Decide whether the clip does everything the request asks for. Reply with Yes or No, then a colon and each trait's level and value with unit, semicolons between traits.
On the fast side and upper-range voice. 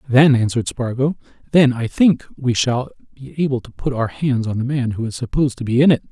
No: fast, 235 wpm; low, 130 Hz